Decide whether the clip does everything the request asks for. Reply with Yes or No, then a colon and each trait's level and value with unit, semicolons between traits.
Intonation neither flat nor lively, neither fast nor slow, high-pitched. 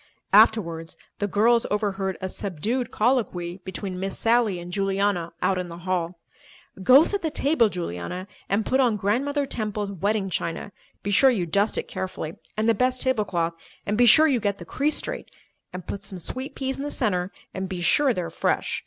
Yes: average, 4.9 semitones; average, 175 wpm; high, 200 Hz